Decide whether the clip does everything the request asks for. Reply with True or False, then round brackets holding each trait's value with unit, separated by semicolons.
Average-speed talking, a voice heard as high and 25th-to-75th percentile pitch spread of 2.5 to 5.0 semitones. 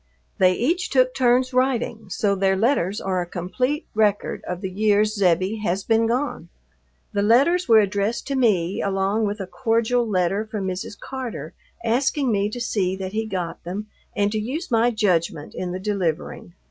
True (175 wpm; 210 Hz; 4.0 semitones)